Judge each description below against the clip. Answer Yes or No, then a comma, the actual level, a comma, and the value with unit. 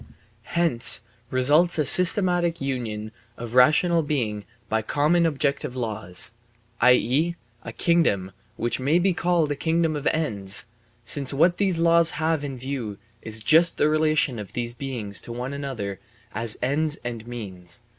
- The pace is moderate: Yes, average, 145 wpm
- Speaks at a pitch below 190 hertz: Yes, low, 135 Hz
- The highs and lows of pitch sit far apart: Yes, wide, 6.0 semitones